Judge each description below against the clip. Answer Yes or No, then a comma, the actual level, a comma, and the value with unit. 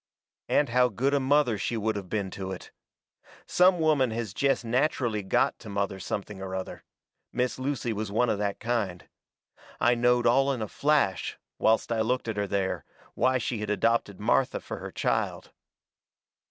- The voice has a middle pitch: No, low, 115 Hz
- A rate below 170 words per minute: No, average, 180 wpm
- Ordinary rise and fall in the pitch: Yes, average, 4.1 semitones